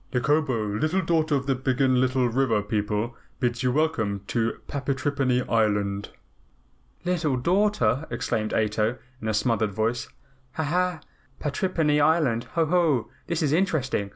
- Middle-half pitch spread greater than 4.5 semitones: Yes, wide, 5.6 semitones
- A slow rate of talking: Yes, slow, 130 wpm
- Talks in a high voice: No, low, 130 Hz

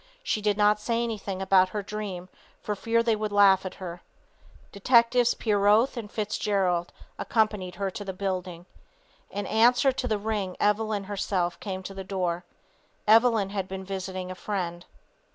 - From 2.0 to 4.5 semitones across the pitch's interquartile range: Yes, narrow, 2.5 semitones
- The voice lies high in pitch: Yes, high, 200 Hz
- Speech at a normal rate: Yes, average, 160 wpm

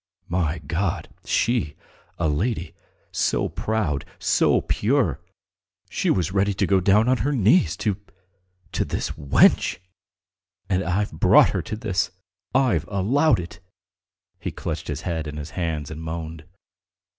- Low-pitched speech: Yes, very low, 90 Hz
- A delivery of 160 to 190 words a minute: No, average, 140 wpm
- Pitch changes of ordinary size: Yes, average, 5.0 semitones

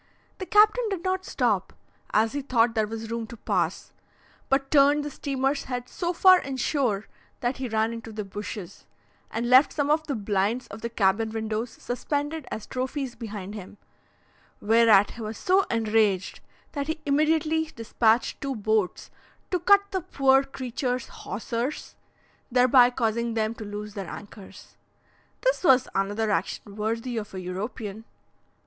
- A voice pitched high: Yes, high, 235 Hz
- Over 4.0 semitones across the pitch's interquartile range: Yes, average, 4.4 semitones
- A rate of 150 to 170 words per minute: Yes, average, 155 wpm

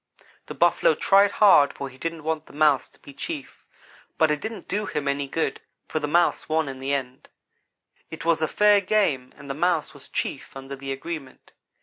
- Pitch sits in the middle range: Yes, medium, 155 Hz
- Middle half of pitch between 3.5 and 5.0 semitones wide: Yes, average, 4.0 semitones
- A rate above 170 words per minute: Yes, fast, 205 wpm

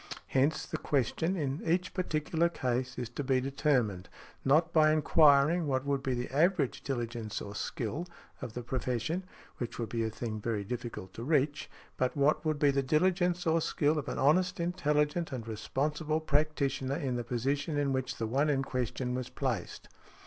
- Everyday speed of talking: Yes, average, 180 wpm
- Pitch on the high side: No, medium, 140 Hz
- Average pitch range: Yes, average, 3.9 semitones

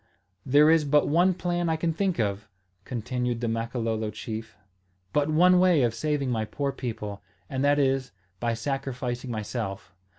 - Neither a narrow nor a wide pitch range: Yes, average, 4.9 semitones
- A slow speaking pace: No, average, 160 wpm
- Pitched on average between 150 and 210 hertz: No, low, 130 Hz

